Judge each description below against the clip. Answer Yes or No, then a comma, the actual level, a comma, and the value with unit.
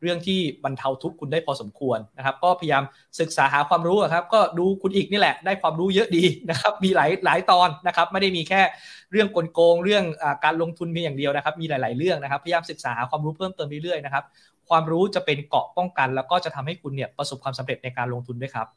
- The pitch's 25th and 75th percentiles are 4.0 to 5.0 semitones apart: Yes, average, 4.5 semitones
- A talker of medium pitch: Yes, medium, 165 Hz